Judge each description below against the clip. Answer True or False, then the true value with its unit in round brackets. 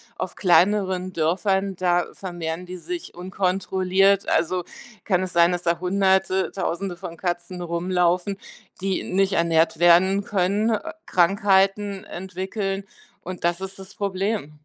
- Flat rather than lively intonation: True (1.8 semitones)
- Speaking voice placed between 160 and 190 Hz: True (185 Hz)